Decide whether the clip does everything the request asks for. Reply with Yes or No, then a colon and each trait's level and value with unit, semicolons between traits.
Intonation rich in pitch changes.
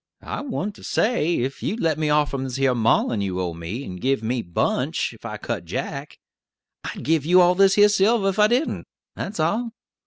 Yes: wide, 8.5 semitones